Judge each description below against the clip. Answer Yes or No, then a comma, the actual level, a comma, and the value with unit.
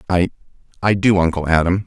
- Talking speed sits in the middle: No, slow, 130 wpm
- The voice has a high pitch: No, very low, 90 Hz